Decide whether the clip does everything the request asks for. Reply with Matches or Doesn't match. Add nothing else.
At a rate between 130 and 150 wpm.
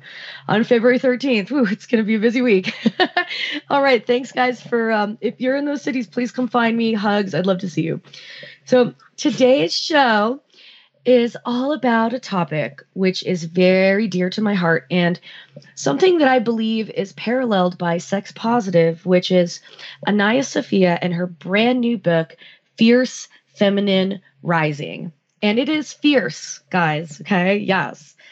Doesn't match